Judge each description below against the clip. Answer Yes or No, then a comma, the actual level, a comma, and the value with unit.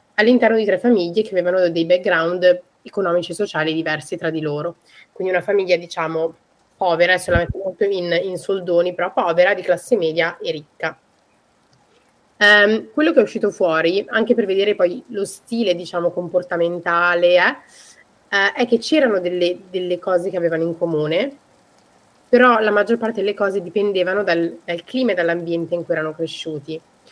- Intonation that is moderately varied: Yes, average, 3.2 semitones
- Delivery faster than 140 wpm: Yes, average, 160 wpm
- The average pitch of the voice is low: No, medium, 180 Hz